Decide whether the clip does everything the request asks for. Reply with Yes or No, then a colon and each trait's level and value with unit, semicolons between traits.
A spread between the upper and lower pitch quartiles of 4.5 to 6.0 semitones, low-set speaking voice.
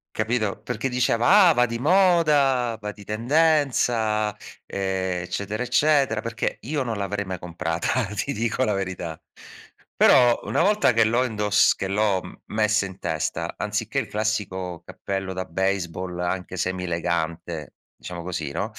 Yes: average, 4.8 semitones; low, 105 Hz